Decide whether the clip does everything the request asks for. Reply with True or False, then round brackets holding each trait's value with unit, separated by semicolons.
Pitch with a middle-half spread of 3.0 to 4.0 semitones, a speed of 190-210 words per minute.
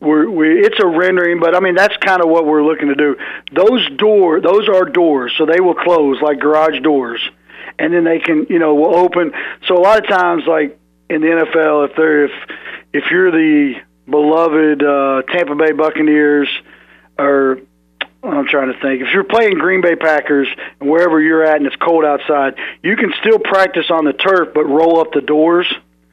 True (3.4 semitones; 200 wpm)